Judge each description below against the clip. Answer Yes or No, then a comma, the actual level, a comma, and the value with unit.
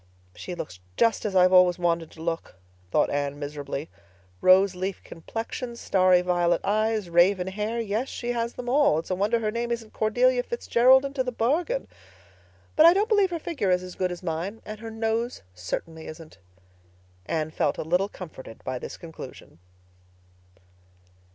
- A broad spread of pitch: Yes, wide, 5.7 semitones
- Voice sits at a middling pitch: No, high, 195 Hz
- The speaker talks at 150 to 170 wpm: Yes, average, 160 wpm